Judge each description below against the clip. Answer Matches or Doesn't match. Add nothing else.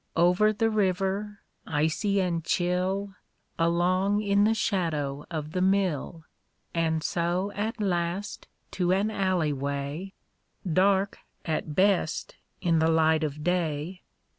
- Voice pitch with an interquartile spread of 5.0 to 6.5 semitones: Doesn't match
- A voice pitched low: Doesn't match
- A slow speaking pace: Matches